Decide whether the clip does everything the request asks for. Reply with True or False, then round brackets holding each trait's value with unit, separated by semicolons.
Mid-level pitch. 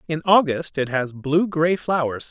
True (155 Hz)